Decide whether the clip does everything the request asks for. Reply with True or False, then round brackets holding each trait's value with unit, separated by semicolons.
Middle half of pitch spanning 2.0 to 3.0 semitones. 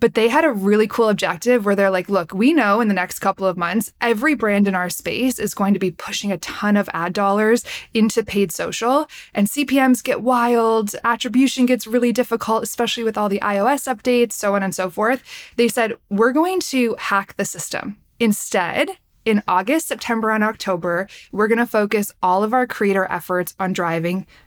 False (3.5 semitones)